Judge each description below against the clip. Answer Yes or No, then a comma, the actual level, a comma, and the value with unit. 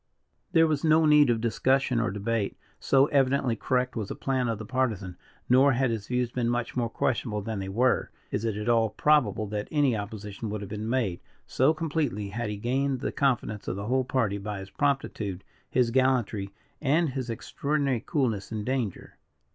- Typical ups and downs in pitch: Yes, average, 4.2 semitones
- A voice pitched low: Yes, low, 120 Hz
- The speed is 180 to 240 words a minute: Yes, average, 190 wpm